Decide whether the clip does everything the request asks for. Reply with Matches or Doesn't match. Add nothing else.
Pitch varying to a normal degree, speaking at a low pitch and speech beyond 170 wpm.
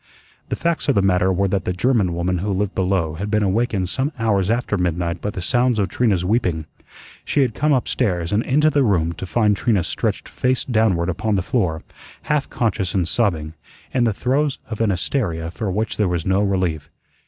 Matches